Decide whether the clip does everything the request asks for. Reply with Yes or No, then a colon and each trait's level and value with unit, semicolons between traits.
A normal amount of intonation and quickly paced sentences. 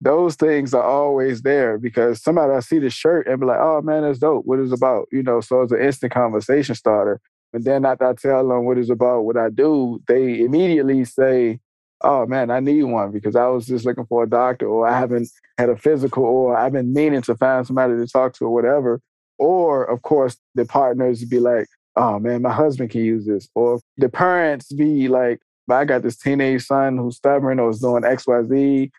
No: narrow, 2.2 semitones; fast, 220 wpm